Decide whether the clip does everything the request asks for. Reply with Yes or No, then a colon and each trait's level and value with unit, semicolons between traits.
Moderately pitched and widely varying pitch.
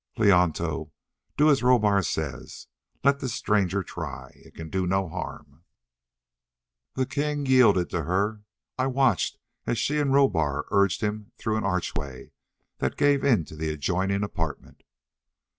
No: low, 100 Hz; wide, 6.9 semitones